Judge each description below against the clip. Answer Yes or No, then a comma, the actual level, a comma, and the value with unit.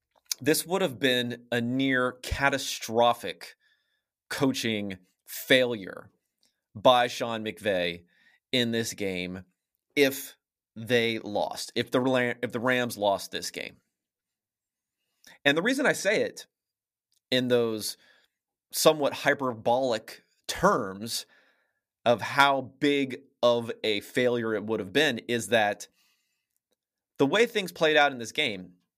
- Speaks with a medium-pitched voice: No, low, 120 Hz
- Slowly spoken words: Yes, slow, 115 wpm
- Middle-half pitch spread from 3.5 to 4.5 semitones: Yes, average, 3.9 semitones